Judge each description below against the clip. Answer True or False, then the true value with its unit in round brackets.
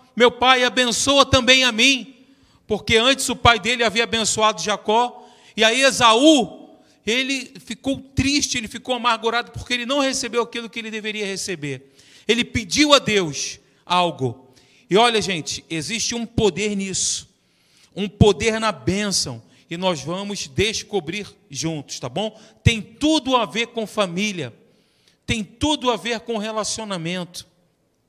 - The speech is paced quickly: False (145 wpm)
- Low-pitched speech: False (220 Hz)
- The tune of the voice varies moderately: True (4.4 semitones)